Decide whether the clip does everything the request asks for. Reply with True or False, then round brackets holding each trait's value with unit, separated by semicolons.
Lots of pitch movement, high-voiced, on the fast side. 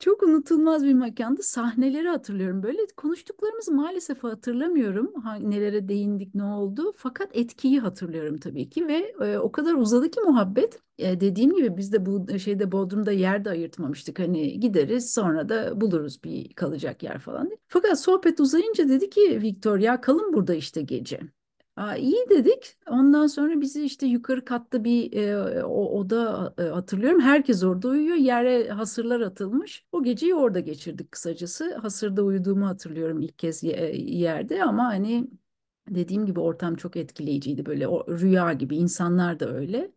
True (7.2 semitones; 235 Hz; 155 wpm)